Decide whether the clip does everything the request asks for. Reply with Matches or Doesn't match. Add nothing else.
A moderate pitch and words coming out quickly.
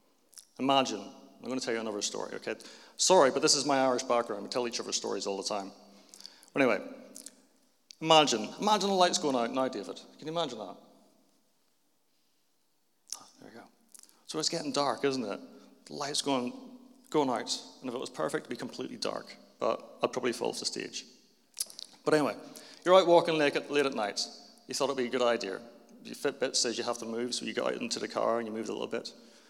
Matches